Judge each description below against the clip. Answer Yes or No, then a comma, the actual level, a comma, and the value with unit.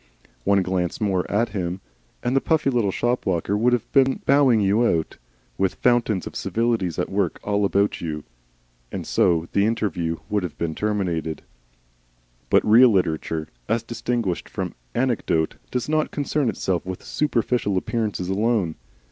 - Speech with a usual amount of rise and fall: Yes, average, 4.9 semitones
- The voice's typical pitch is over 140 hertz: No, low, 105 Hz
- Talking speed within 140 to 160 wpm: Yes, average, 150 wpm